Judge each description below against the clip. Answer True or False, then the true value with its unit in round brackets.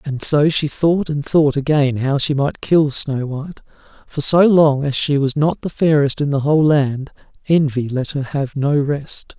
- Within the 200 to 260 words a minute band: True (205 wpm)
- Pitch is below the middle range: False (145 Hz)